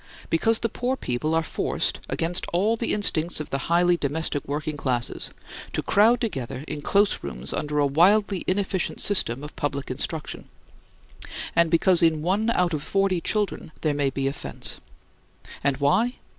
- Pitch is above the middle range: No, medium, 165 Hz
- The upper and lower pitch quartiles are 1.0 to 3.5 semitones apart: No, wide, 5.5 semitones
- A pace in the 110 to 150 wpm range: No, average, 165 wpm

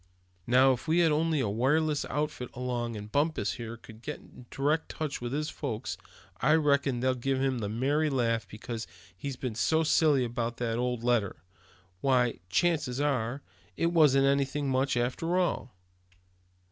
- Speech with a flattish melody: No, average, 3.8 semitones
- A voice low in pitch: Yes, low, 130 Hz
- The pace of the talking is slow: No, average, 165 wpm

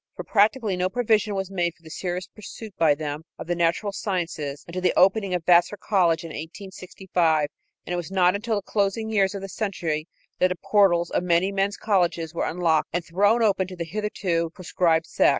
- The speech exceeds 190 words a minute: Yes, fast, 205 wpm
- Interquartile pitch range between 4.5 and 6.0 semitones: No, average, 3.0 semitones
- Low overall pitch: No, medium, 185 Hz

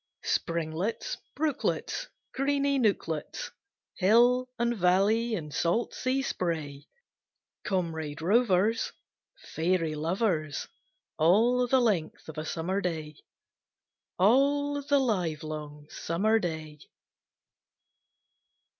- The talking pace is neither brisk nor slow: No, slow, 85 wpm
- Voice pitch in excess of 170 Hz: Yes, medium, 185 Hz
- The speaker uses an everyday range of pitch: No, wide, 7.1 semitones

